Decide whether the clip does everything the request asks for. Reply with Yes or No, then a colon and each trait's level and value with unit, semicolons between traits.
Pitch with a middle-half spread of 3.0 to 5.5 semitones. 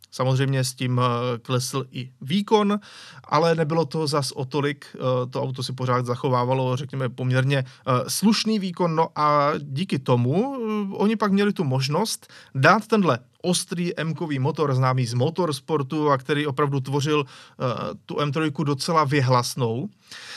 Yes: average, 4.2 semitones